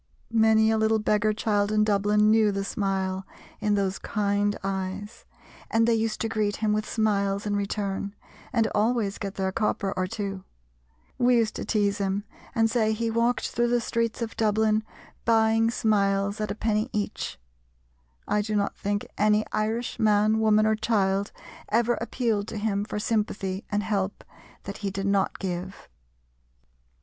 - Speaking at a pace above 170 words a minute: No, average, 165 wpm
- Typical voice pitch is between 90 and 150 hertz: No, high, 210 Hz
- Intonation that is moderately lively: No, narrow, 1.8 semitones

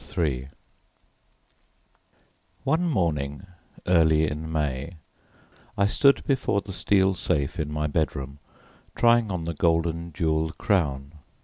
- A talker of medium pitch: No, very low, 80 Hz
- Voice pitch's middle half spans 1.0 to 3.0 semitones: No, average, 4.1 semitones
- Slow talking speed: Yes, slow, 110 wpm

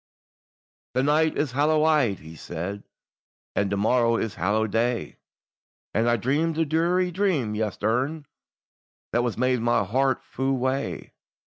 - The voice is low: Yes, low, 125 Hz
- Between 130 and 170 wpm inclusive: Yes, average, 140 wpm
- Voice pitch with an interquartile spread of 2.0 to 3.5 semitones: No, average, 5.1 semitones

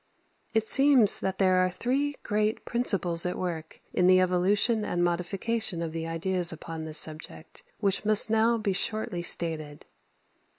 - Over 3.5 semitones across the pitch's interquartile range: Yes, average, 4.2 semitones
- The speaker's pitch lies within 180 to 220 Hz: Yes, medium, 185 Hz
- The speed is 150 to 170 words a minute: Yes, average, 155 wpm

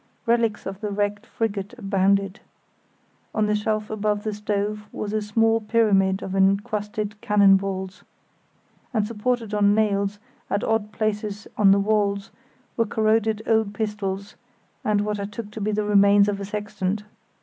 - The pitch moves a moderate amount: No, narrow, 1.3 semitones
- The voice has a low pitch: No, high, 210 Hz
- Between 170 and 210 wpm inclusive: No, average, 155 wpm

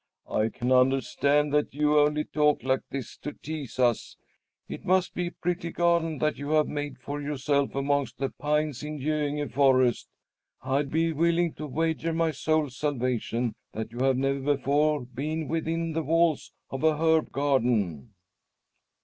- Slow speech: No, average, 160 wpm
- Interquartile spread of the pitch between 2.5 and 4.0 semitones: Yes, average, 2.8 semitones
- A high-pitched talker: No, medium, 145 Hz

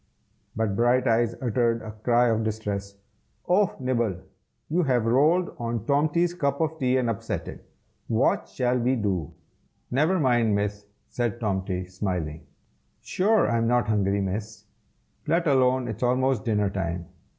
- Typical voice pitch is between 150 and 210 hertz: No, low, 115 Hz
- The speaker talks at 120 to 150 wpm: Yes, average, 140 wpm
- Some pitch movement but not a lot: Yes, average, 4.0 semitones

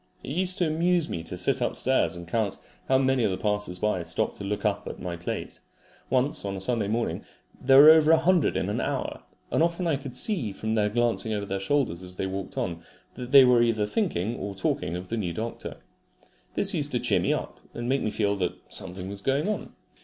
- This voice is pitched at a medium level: No, low, 110 Hz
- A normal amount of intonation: No, wide, 6.0 semitones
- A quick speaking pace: Yes, fast, 225 wpm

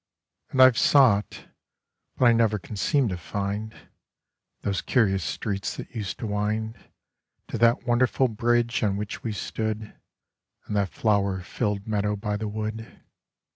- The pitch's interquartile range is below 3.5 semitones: Yes, narrow, 2.4 semitones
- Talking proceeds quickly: No, average, 145 wpm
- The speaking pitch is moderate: No, low, 105 Hz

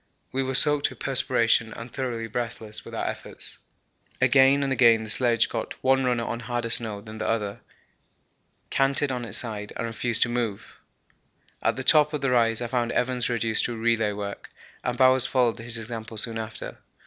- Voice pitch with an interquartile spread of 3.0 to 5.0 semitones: No, narrow, 2.4 semitones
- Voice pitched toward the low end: Yes, low, 120 Hz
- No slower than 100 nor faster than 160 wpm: No, average, 185 wpm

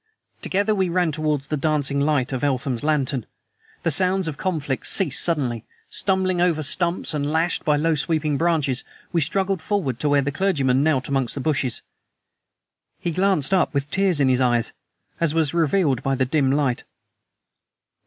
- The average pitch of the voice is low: No, medium, 150 Hz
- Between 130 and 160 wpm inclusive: No, average, 170 wpm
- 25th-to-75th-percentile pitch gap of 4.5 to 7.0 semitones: No, average, 4.0 semitones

